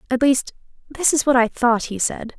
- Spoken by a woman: Yes, female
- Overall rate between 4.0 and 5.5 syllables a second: Yes, 5.0 syllables/s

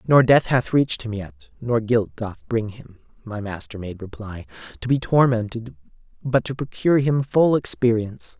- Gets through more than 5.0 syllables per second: No, 4.9 syllables/s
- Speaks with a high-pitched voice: No, low, 120 Hz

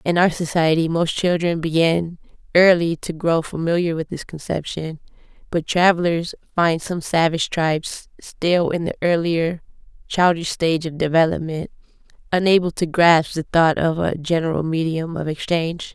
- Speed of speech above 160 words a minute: No, average, 145 wpm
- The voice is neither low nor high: Yes, medium, 165 Hz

